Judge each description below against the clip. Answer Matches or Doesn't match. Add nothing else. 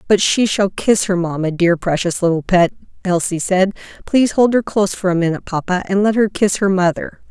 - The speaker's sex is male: Doesn't match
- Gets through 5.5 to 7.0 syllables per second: Matches